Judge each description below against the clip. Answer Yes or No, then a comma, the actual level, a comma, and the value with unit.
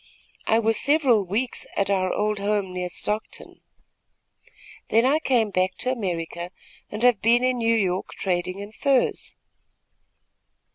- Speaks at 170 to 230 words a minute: No, average, 140 wpm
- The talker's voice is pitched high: Yes, high, 210 Hz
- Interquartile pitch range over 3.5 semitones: Yes, average, 4.3 semitones